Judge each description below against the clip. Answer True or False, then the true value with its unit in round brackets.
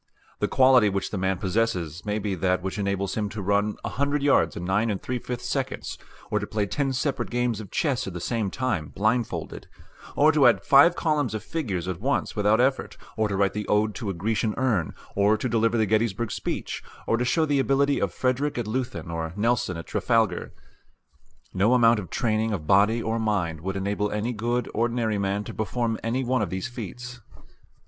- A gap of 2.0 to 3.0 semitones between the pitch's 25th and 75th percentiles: False (3.8 semitones)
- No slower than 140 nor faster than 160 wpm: False (205 wpm)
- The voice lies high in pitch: False (110 Hz)